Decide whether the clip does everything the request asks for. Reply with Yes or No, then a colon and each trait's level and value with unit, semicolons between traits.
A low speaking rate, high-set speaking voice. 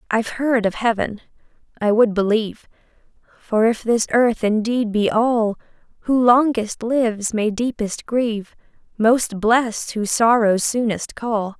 Yes: slow, 130 wpm; high, 225 Hz